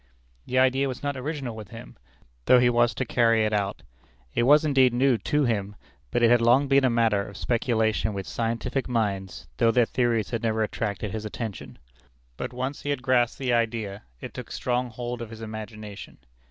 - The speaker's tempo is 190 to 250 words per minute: Yes, average, 200 wpm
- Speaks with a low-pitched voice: Yes, low, 115 Hz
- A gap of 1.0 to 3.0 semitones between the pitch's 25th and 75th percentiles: Yes, average, 2.7 semitones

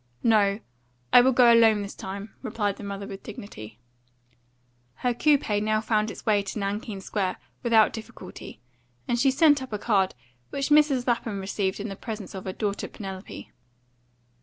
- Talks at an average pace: Yes, average, 165 wpm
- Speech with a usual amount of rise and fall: Yes, average, 3.1 semitones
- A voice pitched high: Yes, high, 215 Hz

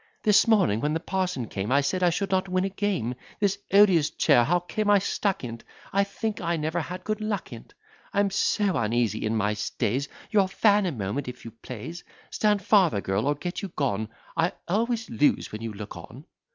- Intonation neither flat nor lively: No, wide, 9.0 semitones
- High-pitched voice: No, medium, 175 Hz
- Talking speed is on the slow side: No, fast, 205 wpm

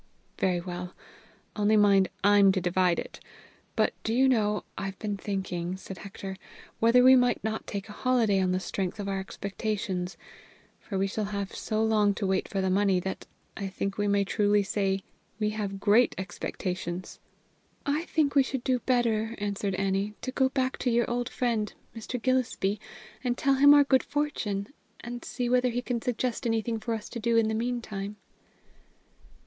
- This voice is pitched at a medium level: No, high, 210 Hz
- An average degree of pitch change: Yes, average, 3.7 semitones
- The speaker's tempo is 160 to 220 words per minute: Yes, average, 185 wpm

